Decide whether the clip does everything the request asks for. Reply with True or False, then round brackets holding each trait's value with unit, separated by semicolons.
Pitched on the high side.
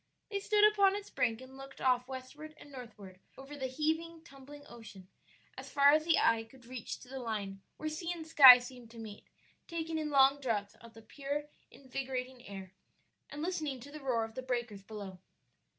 True (260 Hz)